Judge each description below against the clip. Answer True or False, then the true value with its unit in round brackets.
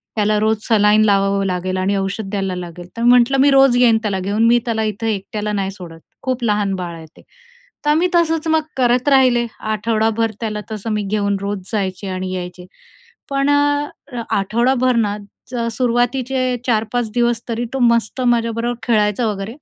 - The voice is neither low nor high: False (220 Hz)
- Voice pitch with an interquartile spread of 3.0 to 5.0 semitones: True (3.5 semitones)